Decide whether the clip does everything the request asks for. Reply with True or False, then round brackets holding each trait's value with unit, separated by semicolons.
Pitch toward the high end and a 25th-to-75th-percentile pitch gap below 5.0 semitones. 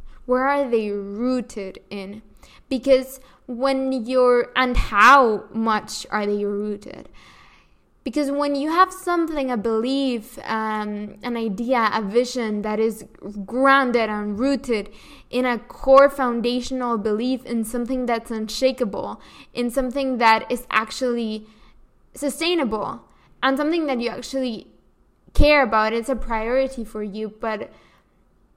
True (245 Hz; 3.4 semitones)